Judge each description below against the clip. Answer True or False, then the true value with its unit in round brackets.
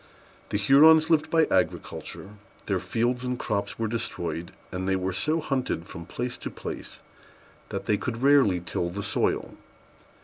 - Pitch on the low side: True (115 Hz)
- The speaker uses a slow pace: False (160 wpm)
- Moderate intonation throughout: False (6.5 semitones)